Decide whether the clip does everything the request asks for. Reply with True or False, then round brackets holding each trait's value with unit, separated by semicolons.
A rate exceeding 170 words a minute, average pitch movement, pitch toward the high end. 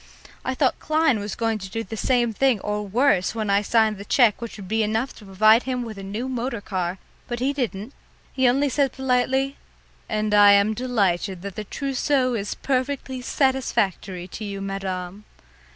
True (185 wpm; 4.3 semitones; 225 Hz)